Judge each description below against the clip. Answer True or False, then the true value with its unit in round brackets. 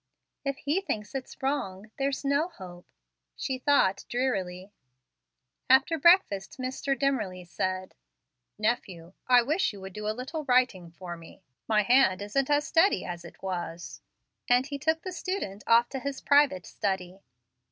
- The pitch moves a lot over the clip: True (6.7 semitones)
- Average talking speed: True (150 wpm)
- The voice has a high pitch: True (240 Hz)